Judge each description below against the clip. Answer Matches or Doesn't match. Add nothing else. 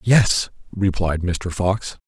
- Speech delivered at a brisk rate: Doesn't match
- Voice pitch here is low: Matches